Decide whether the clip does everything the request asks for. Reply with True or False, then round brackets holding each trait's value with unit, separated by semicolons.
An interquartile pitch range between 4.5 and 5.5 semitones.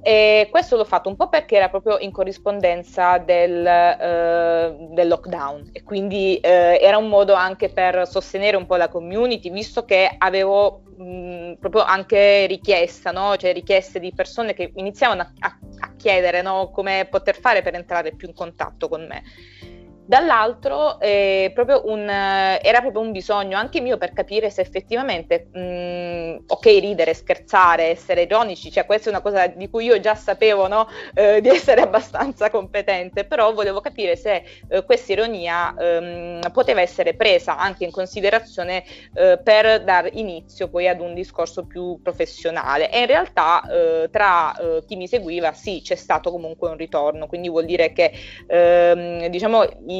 False (3.5 semitones)